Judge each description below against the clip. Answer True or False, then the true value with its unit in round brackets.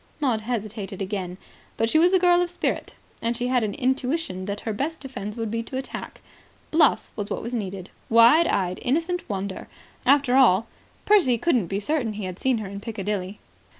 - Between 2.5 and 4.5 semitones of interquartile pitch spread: False (5.2 semitones)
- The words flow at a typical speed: True (185 wpm)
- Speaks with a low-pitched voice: False (230 Hz)